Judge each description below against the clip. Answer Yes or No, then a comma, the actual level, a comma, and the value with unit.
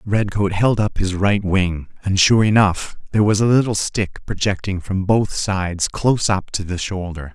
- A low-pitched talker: Yes, low, 100 Hz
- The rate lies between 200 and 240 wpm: No, average, 190 wpm